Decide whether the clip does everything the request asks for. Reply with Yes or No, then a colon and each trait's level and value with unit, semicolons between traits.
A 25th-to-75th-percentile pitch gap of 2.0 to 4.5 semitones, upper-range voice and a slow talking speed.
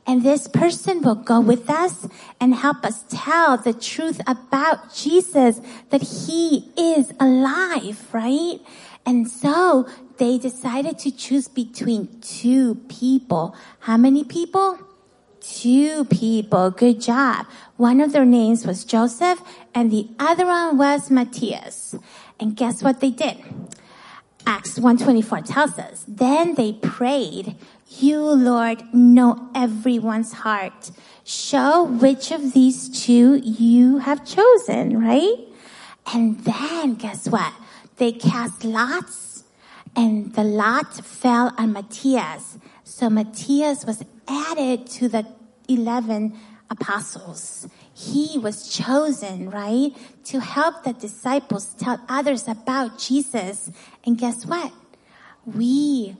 Yes: average, 3.7 semitones; high, 245 Hz; slow, 120 wpm